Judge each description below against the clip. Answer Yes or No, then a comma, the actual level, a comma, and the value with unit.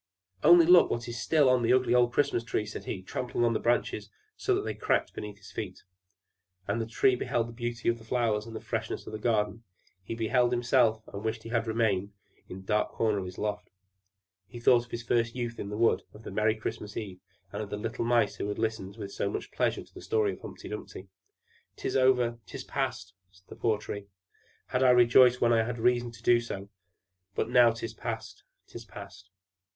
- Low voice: Yes, low, 115 Hz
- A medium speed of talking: No, fast, 230 wpm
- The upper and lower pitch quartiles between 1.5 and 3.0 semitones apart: Yes, narrow, 2.4 semitones